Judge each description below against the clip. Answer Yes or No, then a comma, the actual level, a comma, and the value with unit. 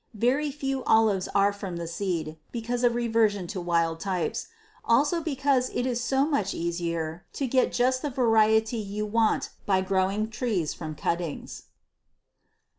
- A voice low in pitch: No, high, 215 Hz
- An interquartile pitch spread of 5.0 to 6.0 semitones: Yes, average, 5.3 semitones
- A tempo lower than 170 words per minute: Yes, average, 150 wpm